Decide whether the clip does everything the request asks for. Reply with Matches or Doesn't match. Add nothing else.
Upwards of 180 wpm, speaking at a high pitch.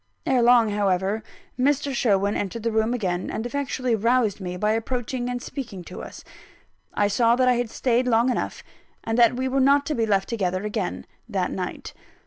Matches